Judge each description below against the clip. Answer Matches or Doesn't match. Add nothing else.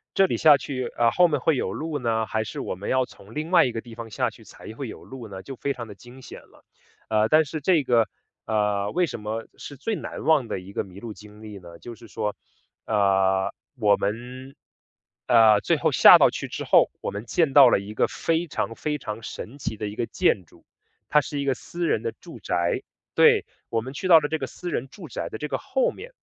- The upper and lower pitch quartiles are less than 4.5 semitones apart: Doesn't match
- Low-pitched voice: Matches